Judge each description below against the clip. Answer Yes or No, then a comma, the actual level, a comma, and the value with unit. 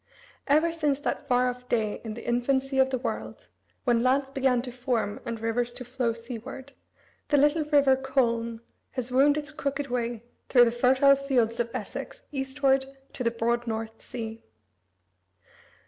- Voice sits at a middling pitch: No, very high, 255 Hz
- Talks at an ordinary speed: Yes, average, 160 wpm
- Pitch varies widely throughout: No, narrow, 2.6 semitones